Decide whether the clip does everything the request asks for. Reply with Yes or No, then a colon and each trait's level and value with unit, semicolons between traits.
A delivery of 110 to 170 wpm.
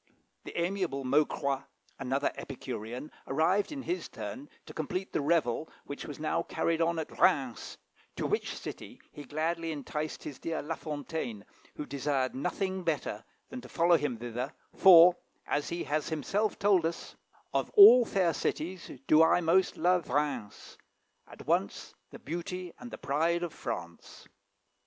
Yes: average, 155 wpm